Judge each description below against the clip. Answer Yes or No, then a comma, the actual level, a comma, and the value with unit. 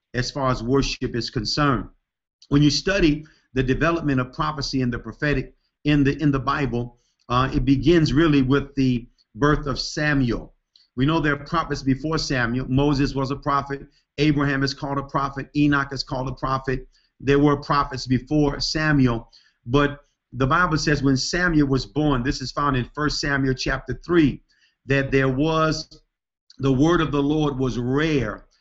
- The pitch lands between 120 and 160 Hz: Yes, medium, 140 Hz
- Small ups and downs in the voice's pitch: Yes, narrow, 2.2 semitones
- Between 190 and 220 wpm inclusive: No, average, 170 wpm